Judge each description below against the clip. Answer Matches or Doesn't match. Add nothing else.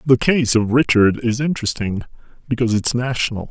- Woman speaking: Doesn't match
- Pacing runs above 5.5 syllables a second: Matches